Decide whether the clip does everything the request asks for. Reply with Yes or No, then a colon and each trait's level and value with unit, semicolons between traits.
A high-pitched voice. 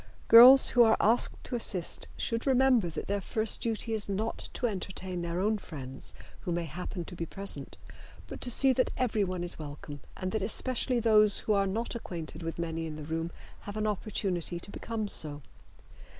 Yes: high, 200 Hz